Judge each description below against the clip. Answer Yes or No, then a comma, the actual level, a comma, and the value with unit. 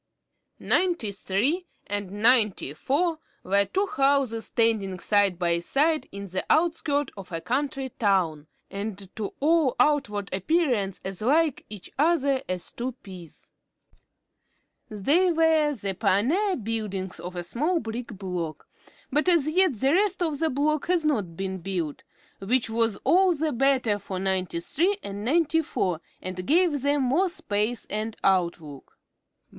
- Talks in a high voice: Yes, high, 230 Hz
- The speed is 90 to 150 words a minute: Yes, average, 145 wpm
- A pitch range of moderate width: No, wide, 7.9 semitones